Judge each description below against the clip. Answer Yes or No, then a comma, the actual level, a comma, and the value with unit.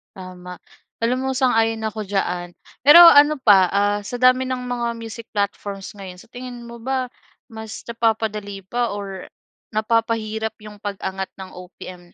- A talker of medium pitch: No, high, 220 Hz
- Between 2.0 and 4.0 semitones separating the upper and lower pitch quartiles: Yes, average, 3.5 semitones